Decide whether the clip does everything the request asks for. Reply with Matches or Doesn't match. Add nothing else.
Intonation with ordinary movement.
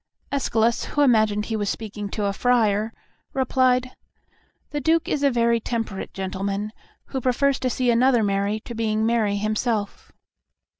Matches